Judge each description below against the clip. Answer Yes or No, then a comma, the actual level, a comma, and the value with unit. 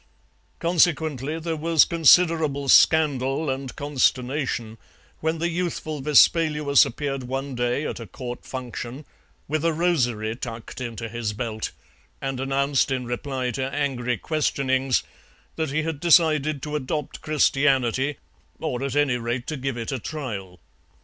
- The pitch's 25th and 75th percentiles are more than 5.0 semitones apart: No, average, 3.7 semitones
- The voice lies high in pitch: No, low, 135 Hz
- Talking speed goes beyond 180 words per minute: No, slow, 135 wpm